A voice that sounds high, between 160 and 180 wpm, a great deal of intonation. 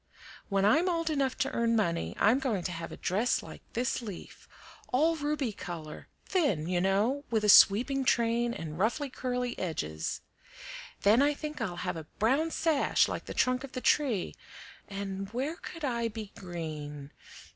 Yes: high, 230 Hz; average, 170 wpm; wide, 6.4 semitones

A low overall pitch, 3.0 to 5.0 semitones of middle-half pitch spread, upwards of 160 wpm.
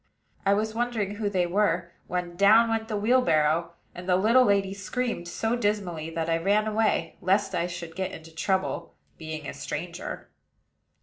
No: high, 195 Hz; average, 4.0 semitones; average, 170 wpm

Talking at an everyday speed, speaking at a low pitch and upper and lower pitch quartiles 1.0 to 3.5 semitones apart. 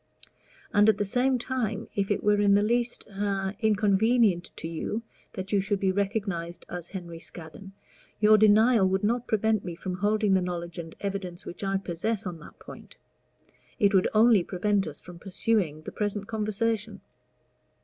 No: average, 170 wpm; high, 200 Hz; average, 2.8 semitones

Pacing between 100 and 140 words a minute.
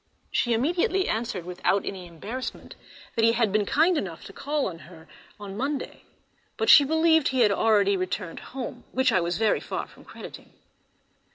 No: average, 175 wpm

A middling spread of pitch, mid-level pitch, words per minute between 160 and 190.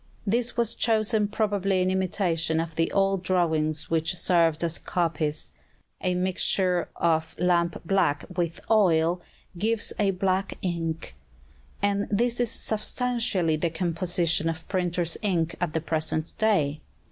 No: average, 3.4 semitones; medium, 180 Hz; slow, 135 wpm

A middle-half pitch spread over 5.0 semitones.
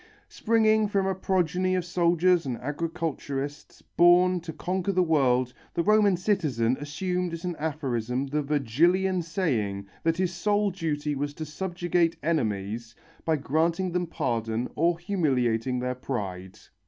Yes: wide, 5.5 semitones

